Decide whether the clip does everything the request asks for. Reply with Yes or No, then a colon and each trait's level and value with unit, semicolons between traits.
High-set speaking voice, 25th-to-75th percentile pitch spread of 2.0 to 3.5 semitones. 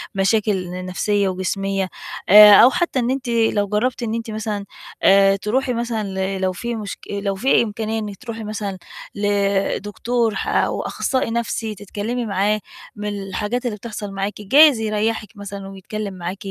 Yes: high, 210 Hz; narrow, 2.5 semitones